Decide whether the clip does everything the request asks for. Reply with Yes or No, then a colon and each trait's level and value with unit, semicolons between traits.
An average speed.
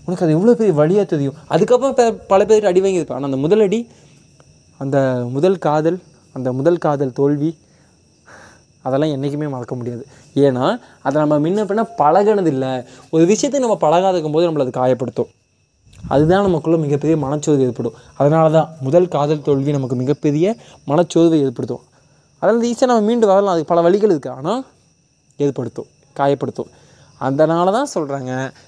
No: fast, 150 wpm